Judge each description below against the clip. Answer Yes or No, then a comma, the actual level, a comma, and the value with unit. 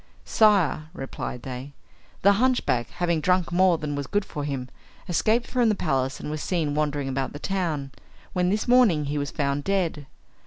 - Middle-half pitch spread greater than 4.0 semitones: Yes, average, 5.1 semitones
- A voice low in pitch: No, medium, 155 Hz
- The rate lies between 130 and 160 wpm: No, average, 180 wpm